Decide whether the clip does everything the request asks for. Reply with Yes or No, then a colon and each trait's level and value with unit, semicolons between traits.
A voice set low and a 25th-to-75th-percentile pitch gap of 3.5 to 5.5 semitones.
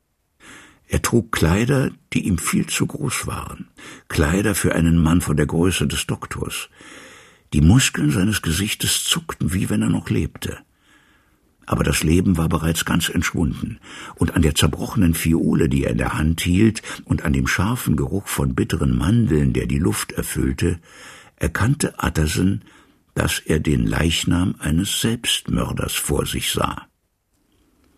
Yes: very low, 85 Hz; average, 3.8 semitones